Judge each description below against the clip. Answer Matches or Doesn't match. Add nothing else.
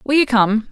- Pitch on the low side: Doesn't match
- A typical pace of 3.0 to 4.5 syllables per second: Doesn't match